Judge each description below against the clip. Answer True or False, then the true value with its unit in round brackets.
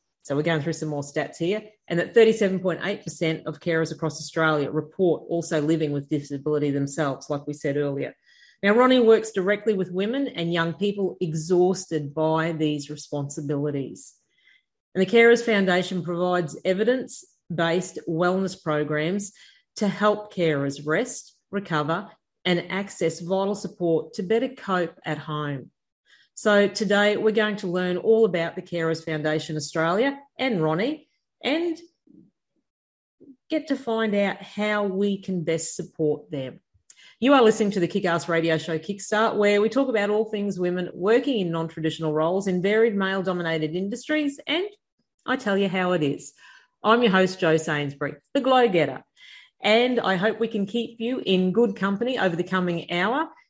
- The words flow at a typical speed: True (155 wpm)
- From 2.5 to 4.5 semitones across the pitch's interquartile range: False (5.3 semitones)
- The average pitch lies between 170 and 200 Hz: True (185 Hz)